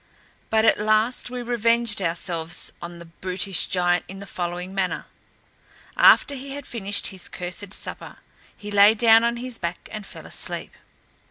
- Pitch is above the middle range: Yes, high, 205 Hz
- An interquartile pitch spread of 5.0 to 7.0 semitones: No, average, 4.5 semitones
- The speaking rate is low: No, average, 160 wpm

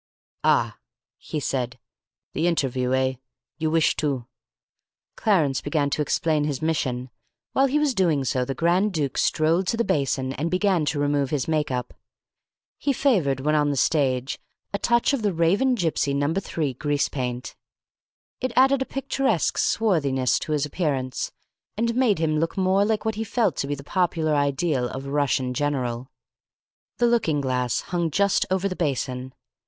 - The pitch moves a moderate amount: No, wide, 5.9 semitones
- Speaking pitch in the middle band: Yes, medium, 150 Hz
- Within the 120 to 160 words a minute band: No, average, 170 wpm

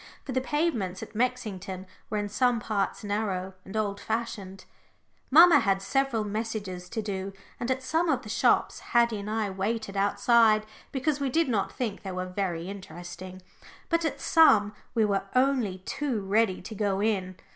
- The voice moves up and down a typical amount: Yes, average, 4.2 semitones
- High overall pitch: Yes, high, 215 Hz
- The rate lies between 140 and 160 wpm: No, average, 170 wpm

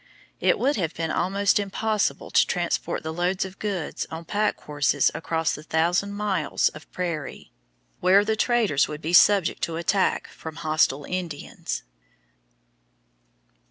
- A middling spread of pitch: Yes, average, 4.1 semitones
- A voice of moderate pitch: Yes, medium, 175 Hz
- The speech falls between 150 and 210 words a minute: No, average, 140 wpm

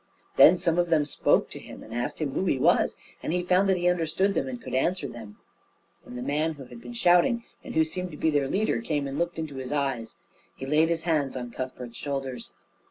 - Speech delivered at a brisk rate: Yes, fast, 235 wpm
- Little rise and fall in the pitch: No, average, 4.8 semitones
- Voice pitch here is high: No, medium, 155 Hz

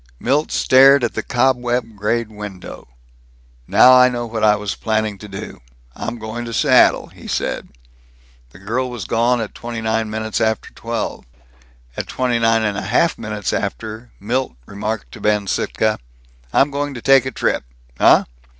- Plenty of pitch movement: No, narrow, 2.6 semitones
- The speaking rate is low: No, average, 170 wpm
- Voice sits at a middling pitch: No, low, 115 Hz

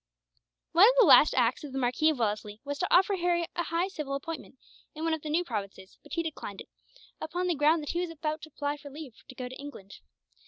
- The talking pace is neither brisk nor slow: No, fast, 245 wpm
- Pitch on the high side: Yes, very high, 305 Hz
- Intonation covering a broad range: No, average, 4.3 semitones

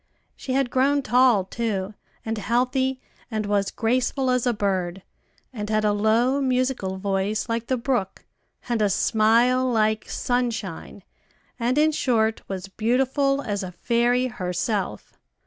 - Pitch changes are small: No, average, 3.7 semitones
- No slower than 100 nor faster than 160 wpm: Yes, average, 140 wpm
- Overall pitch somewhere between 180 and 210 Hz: No, high, 230 Hz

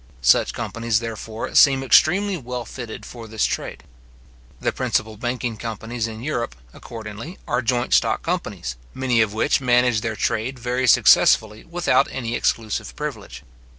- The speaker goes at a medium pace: Yes, average, 145 wpm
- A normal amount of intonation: No, narrow, 2.3 semitones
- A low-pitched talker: Yes, low, 120 Hz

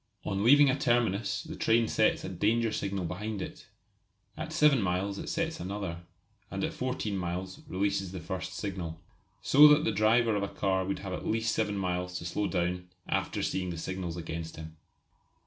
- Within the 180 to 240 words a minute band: Yes, average, 190 wpm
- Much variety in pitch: No, average, 3.8 semitones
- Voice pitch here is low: Yes, very low, 95 Hz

